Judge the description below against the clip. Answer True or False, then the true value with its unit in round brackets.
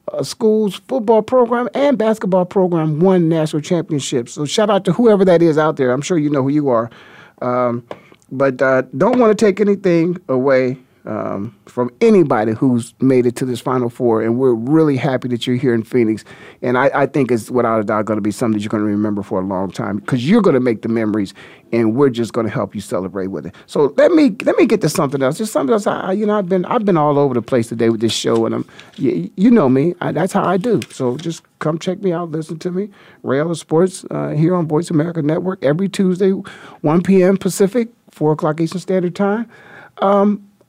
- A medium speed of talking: False (235 wpm)